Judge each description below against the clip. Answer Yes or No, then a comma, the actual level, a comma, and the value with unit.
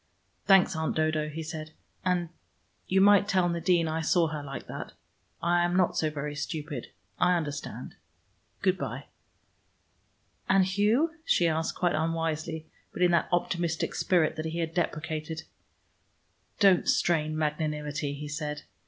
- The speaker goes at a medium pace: Yes, average, 145 wpm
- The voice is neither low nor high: Yes, medium, 160 Hz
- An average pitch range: No, narrow, 2.3 semitones